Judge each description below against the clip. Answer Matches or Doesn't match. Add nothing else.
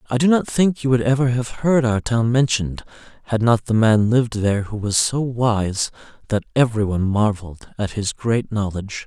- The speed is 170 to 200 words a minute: Matches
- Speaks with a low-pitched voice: Matches